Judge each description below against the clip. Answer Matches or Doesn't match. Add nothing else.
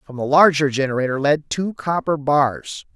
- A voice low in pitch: Doesn't match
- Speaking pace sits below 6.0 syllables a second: Matches